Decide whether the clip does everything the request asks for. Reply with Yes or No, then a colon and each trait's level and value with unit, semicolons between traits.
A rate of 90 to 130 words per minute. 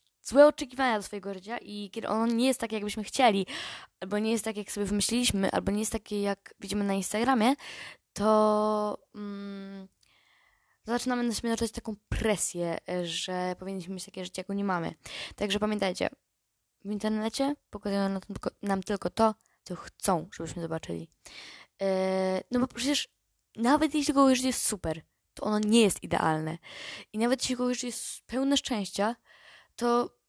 No: average, 155 wpm